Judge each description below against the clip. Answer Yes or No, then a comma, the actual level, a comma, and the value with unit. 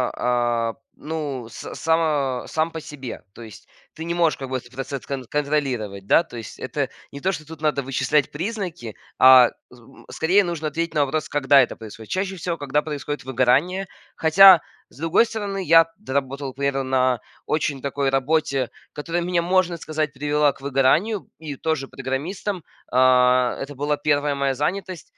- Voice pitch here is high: No, medium, 145 Hz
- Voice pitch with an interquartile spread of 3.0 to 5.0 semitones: Yes, average, 3.9 semitones